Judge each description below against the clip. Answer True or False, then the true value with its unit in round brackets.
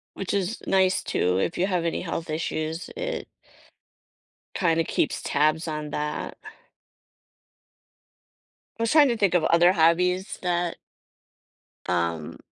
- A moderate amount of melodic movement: True (3.2 semitones)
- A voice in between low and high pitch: True (170 Hz)